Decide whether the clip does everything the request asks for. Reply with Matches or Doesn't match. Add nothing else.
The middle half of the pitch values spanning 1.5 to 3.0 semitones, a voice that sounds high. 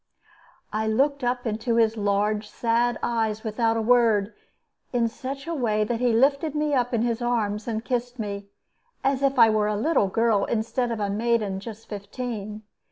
Matches